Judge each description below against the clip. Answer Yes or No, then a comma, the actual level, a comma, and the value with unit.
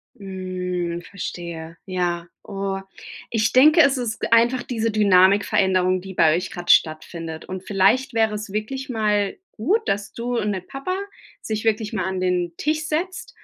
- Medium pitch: No, high, 200 Hz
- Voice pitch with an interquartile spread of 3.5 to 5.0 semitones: Yes, average, 4.2 semitones